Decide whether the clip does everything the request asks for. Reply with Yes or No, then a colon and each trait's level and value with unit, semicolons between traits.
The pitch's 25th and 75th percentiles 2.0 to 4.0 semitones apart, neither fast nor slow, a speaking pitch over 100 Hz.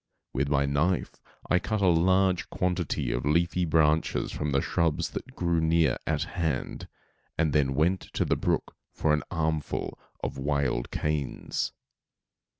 No: average, 3.2 semitones; average, 150 wpm; very low, 80 Hz